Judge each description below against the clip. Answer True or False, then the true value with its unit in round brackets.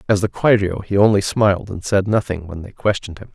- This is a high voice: False (100 Hz)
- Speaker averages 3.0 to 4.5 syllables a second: False (6.1 syllables/s)